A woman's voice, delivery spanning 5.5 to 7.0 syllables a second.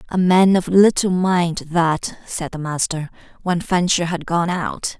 No: female; 3.9 syllables/s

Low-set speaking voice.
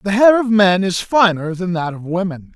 No: high, 190 Hz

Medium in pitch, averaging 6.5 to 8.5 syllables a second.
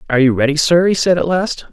Yes: medium, 160 Hz; 6.8 syllables/s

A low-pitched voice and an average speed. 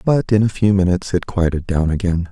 No: very low, 95 Hz; fast, 235 wpm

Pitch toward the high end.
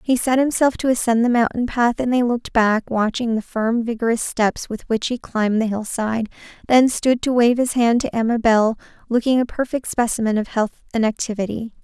Yes: high, 235 Hz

